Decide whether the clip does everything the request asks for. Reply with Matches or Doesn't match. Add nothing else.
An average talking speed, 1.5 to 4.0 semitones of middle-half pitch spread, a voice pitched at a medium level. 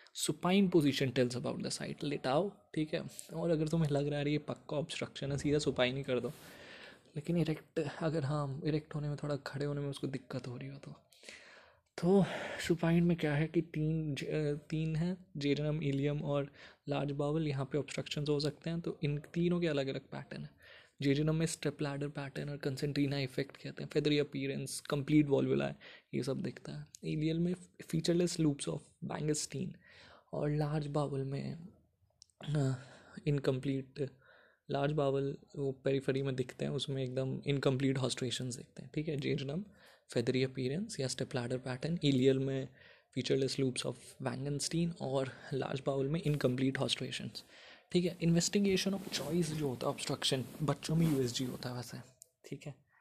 Matches